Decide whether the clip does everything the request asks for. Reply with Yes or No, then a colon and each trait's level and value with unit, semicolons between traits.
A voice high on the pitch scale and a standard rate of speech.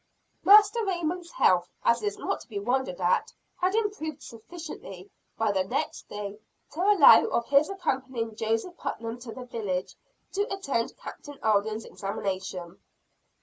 Yes: high, 235 Hz; average, 145 wpm